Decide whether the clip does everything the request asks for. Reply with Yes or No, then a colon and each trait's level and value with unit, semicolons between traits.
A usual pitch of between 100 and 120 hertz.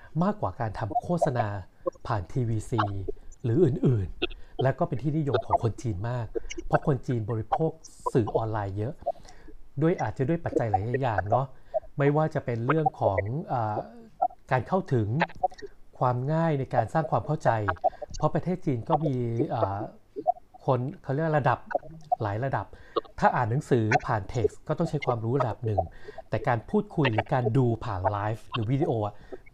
No: low, 135 Hz